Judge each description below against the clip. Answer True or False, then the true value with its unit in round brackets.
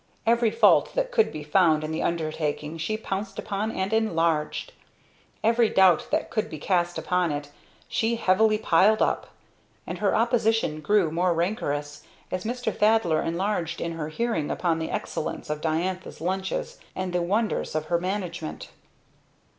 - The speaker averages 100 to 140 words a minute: False (155 wpm)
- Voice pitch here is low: False (180 Hz)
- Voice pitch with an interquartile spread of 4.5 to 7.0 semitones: True (5.1 semitones)